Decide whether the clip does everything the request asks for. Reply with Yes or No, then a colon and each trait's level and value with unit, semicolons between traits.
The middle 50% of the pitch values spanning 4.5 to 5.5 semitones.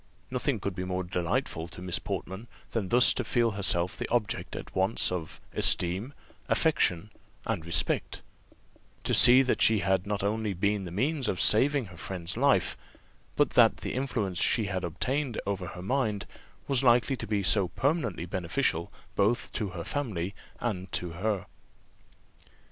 Yes: average, 4.9 semitones